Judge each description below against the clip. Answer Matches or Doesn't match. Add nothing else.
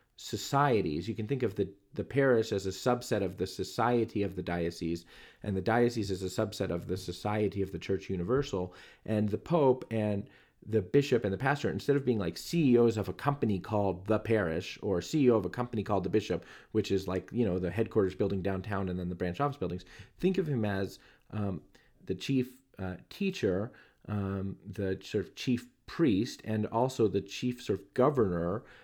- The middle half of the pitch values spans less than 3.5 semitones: Doesn't match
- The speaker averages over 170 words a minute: Matches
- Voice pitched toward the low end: Matches